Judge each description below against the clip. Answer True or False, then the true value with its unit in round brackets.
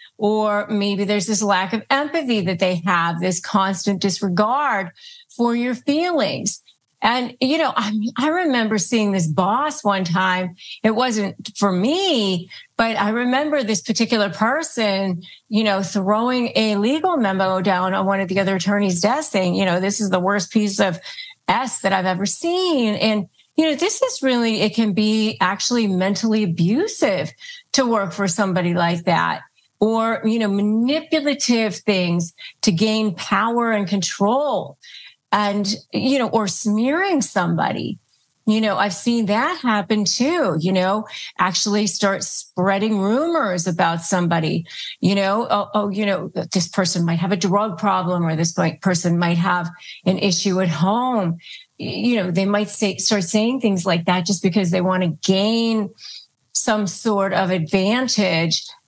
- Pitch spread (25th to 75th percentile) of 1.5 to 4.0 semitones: True (3.5 semitones)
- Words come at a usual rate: True (160 wpm)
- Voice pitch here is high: True (205 Hz)